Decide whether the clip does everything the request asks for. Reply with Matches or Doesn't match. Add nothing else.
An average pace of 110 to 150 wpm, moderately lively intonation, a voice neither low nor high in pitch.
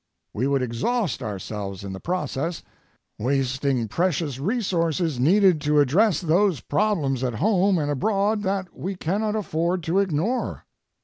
Doesn't match